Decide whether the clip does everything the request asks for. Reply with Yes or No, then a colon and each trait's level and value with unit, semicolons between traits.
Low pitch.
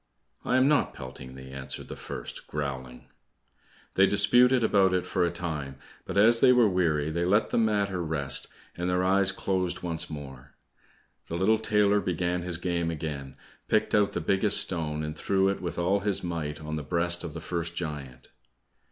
Yes: very low, 85 Hz